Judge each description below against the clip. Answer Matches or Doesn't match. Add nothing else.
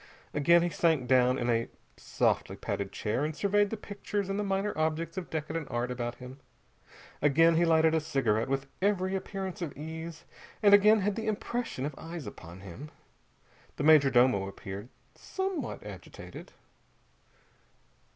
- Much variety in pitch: Matches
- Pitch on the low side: Doesn't match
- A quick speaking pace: Doesn't match